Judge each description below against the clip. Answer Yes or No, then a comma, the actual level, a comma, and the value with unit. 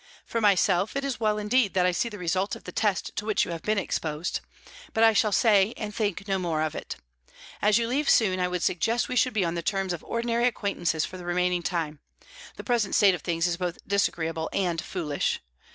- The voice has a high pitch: Yes, high, 195 Hz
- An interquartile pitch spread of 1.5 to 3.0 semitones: No, average, 3.8 semitones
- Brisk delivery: Yes, fast, 230 wpm